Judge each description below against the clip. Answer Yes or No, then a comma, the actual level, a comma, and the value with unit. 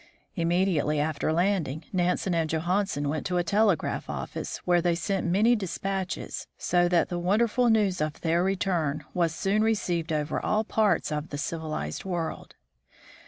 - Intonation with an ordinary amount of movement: Yes, average, 3.5 semitones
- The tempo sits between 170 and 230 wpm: No, average, 155 wpm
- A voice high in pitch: No, medium, 175 Hz